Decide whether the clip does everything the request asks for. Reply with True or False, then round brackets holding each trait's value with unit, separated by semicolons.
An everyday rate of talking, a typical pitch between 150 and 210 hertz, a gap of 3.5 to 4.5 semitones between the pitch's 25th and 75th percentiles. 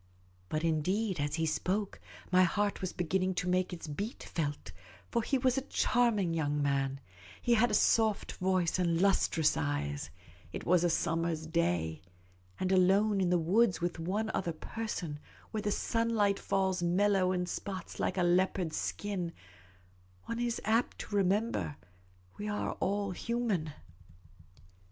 True (155 wpm; 185 Hz; 3.9 semitones)